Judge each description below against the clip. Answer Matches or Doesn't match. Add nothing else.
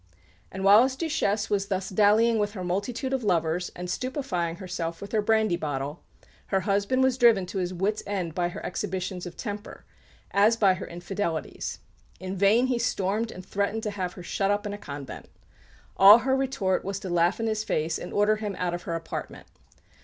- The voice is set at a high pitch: Matches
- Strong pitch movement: Doesn't match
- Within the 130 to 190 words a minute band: Doesn't match